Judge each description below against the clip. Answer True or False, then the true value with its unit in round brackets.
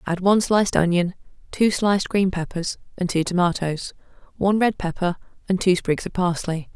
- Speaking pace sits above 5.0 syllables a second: True (5.4 syllables/s)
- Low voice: False (185 Hz)